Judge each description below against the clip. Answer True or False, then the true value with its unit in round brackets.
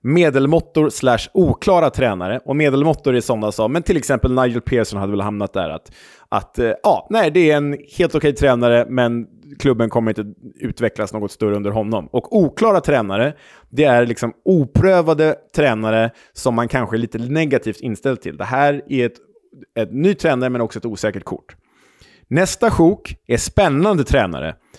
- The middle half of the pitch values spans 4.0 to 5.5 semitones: True (4.9 semitones)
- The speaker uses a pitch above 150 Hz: False (125 Hz)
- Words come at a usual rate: True (170 wpm)